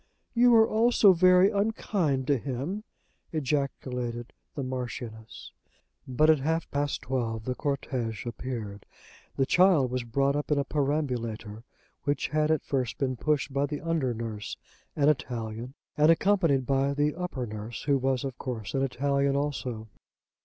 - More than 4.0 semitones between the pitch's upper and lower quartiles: No, average, 3.7 semitones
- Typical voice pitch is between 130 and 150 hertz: Yes, low, 135 Hz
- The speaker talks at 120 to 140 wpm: No, average, 155 wpm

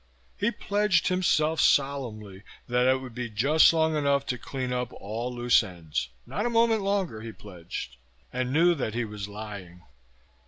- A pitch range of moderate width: No, wide, 6.8 semitones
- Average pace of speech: Yes, average, 165 wpm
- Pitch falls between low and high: No, low, 125 Hz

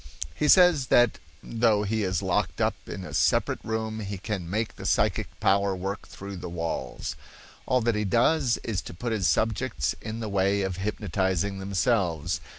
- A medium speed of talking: Yes, average, 175 wpm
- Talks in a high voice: No, low, 100 Hz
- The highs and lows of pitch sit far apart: No, average, 3.1 semitones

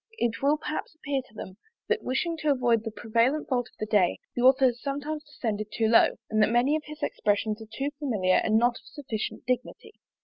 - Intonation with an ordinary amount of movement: Yes, average, 4.7 semitones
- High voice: Yes, high, 245 Hz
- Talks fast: Yes, fast, 215 wpm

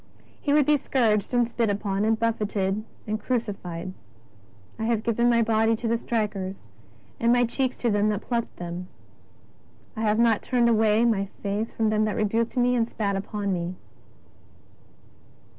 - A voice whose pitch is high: Yes, high, 220 Hz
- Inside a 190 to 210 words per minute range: No, average, 175 wpm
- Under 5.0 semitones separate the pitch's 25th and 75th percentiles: Yes, narrow, 2.5 semitones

